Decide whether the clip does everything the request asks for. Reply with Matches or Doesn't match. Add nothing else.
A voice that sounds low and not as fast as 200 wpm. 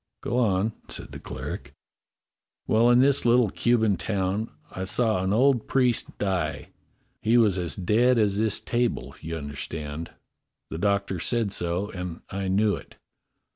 Matches